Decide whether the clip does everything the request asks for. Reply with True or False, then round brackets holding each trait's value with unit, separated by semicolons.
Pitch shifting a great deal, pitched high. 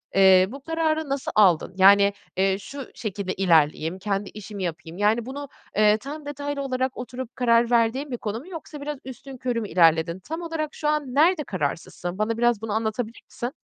True (6.2 semitones; 230 Hz)